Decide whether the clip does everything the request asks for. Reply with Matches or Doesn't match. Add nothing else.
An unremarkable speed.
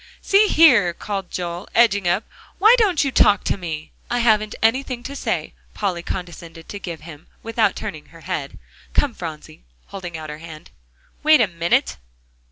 Matches